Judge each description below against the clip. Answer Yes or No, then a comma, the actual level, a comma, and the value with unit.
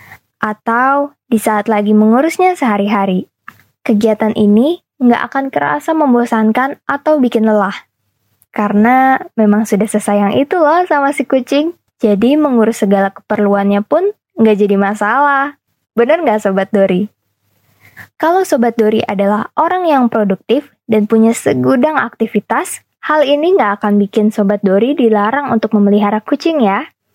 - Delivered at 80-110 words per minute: No, average, 130 wpm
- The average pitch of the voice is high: Yes, high, 220 Hz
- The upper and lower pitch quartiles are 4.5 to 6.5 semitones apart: Yes, average, 5.2 semitones